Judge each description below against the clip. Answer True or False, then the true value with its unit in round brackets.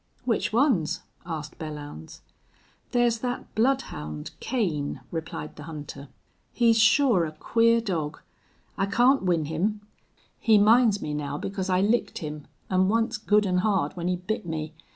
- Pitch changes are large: True (6.7 semitones)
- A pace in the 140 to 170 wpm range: True (150 wpm)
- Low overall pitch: False (190 Hz)